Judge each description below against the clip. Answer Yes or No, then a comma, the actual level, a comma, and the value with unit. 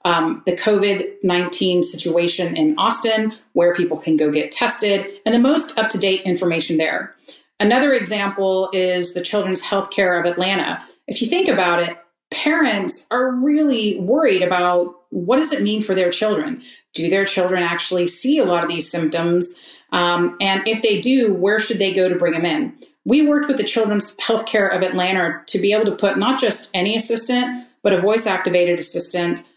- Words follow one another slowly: No, average, 180 wpm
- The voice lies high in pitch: Yes, high, 195 Hz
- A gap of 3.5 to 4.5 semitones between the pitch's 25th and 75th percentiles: Yes, average, 4.0 semitones